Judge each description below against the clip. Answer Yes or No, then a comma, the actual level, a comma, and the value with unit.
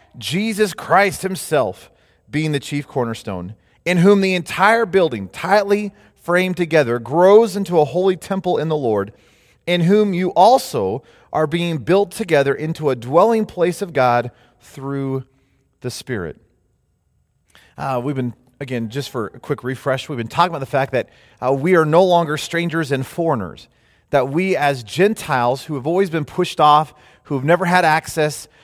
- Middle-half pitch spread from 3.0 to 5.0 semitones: No, wide, 5.5 semitones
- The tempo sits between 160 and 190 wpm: Yes, average, 165 wpm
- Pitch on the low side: No, medium, 155 Hz